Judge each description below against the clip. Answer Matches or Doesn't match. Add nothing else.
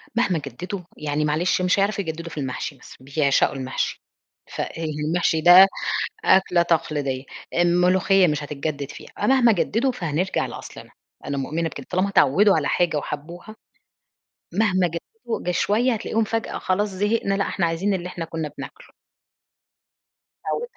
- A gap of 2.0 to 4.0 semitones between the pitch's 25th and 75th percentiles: Doesn't match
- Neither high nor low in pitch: Matches